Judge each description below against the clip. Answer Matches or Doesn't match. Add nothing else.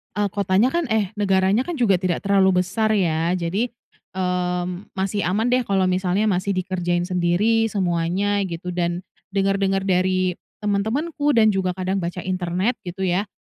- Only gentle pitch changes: Matches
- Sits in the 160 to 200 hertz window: Matches